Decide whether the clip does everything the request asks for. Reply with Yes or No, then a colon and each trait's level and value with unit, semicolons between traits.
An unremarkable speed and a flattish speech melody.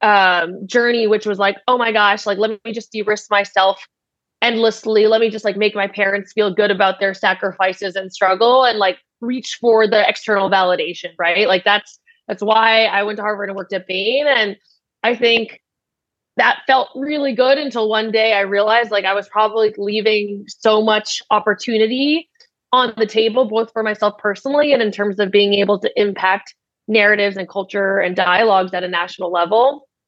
Yes: average, 185 wpm; narrow, 2.3 semitones